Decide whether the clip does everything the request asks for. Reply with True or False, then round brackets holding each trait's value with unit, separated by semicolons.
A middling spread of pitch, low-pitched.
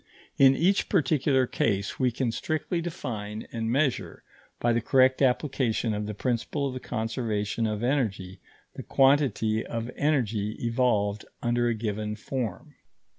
True (3.8 semitones; 120 Hz)